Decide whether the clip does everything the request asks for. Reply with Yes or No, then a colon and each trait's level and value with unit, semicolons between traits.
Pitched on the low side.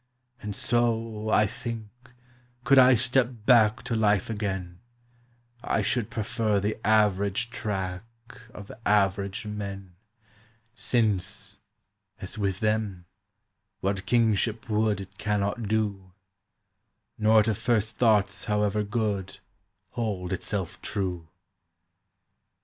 Yes: low, 105 Hz